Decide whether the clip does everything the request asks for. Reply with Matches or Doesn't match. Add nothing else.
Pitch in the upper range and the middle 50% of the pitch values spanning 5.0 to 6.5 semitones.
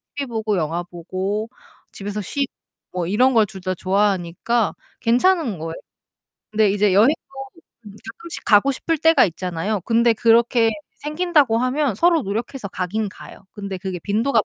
Doesn't match